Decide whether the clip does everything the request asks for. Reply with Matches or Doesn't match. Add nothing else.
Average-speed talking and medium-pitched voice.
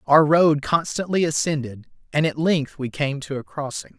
Matches